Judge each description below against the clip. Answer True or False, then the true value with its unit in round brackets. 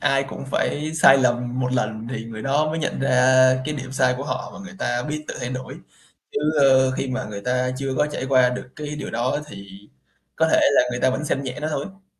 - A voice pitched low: True (130 Hz)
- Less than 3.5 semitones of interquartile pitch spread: True (3.0 semitones)